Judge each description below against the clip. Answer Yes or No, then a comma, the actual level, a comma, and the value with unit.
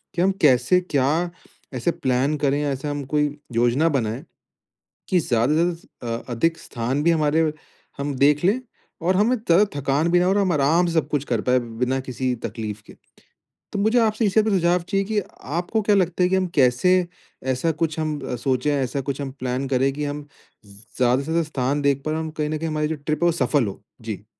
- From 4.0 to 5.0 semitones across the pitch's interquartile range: Yes, average, 4.7 semitones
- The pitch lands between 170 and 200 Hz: No, medium, 150 Hz